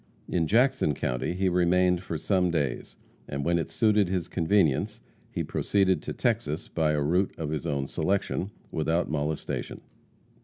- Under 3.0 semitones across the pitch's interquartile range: No, average, 3.9 semitones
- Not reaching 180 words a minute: Yes, average, 155 wpm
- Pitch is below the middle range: Yes, very low, 85 Hz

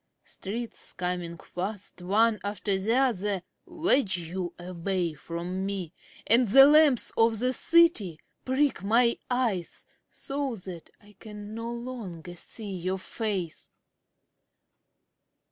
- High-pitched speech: Yes, high, 205 Hz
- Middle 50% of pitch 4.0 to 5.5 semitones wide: Yes, average, 4.8 semitones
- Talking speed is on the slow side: Yes, slow, 115 wpm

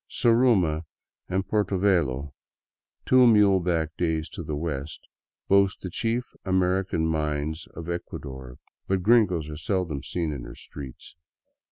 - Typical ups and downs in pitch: Yes, average, 4.2 semitones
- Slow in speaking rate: Yes, slow, 130 wpm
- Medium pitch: No, very low, 85 Hz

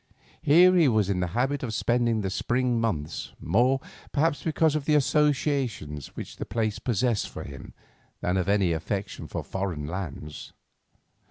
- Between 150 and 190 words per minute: Yes, average, 160 wpm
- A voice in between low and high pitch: No, low, 110 Hz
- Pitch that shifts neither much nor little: No, wide, 6.8 semitones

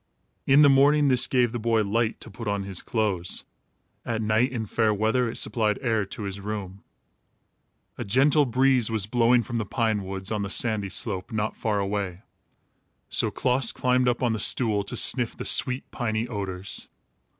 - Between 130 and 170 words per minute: No, average, 185 wpm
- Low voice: Yes, low, 110 Hz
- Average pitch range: Yes, average, 3.4 semitones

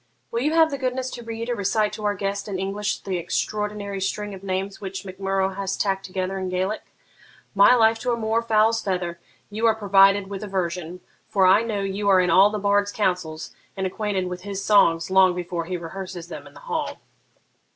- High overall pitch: Yes, high, 195 Hz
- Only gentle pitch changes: Yes, narrow, 2.2 semitones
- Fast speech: Yes, fast, 215 wpm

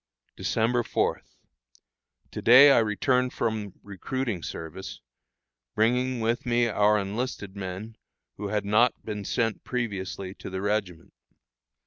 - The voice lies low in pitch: Yes, low, 110 Hz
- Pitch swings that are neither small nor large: Yes, average, 3.3 semitones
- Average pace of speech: No, slow, 120 wpm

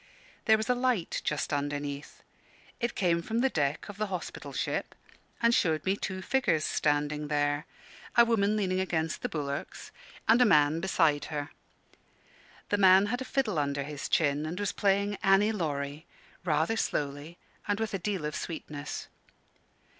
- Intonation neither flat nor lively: No, wide, 5.7 semitones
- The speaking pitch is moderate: Yes, medium, 170 Hz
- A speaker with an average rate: Yes, average, 160 wpm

